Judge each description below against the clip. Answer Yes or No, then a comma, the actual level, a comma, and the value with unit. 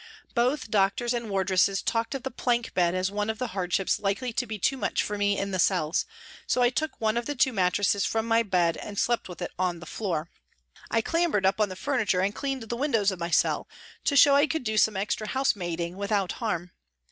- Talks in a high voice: Yes, high, 210 Hz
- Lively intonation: No, average, 4.2 semitones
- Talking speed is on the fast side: Yes, fast, 230 wpm